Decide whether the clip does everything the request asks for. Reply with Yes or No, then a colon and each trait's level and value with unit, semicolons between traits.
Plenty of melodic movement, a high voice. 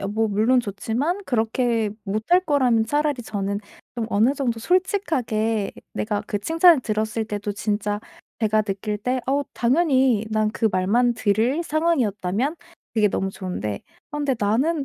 No: average, 4.7 semitones; high, 225 Hz